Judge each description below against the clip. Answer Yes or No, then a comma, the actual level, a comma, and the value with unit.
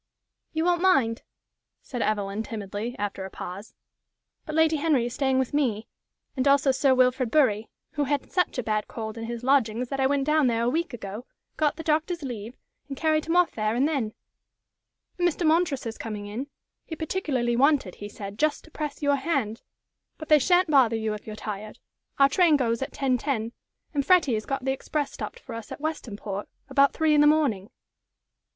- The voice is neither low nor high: No, very high, 265 Hz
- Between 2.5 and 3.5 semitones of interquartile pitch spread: No, wide, 5.4 semitones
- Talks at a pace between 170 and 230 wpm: Yes, average, 195 wpm